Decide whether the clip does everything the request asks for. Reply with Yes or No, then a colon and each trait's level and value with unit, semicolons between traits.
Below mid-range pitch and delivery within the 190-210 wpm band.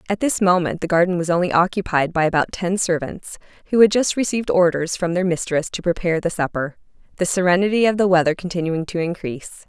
No: medium, 180 Hz; average, 200 wpm